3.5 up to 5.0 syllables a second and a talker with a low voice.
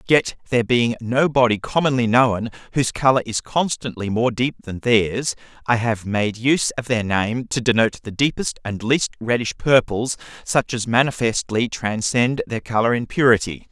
Yes: 4.9 syllables/s; low, 120 Hz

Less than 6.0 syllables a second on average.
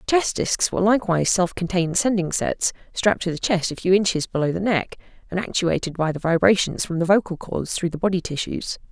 No: 6.1 syllables/s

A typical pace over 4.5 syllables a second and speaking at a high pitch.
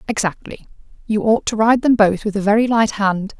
Yes: 5.3 syllables/s; high, 215 Hz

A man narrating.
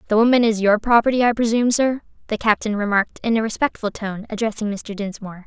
No: female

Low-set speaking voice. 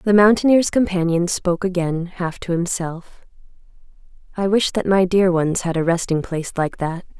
No: medium, 180 Hz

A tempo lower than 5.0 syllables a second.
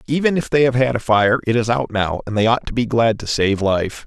No: 5.6 syllables/s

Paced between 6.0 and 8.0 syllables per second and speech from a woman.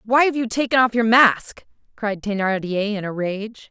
No: 4.6 syllables/s; female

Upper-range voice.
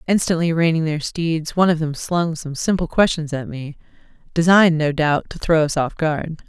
No: medium, 160 Hz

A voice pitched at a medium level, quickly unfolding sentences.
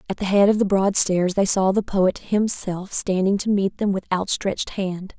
No: high, 195 Hz; fast, 220 wpm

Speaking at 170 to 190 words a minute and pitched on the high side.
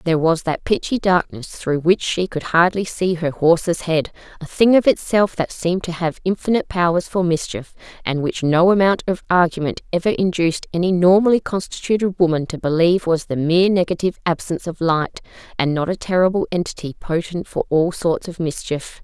No: average, 180 wpm; medium, 175 Hz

